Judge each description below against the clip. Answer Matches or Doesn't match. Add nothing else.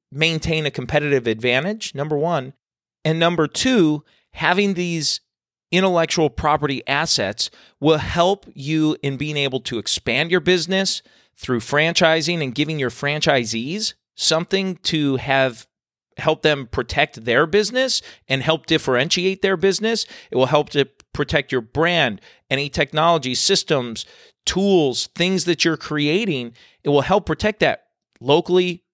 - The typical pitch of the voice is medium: Matches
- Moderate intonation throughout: Matches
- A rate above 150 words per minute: Doesn't match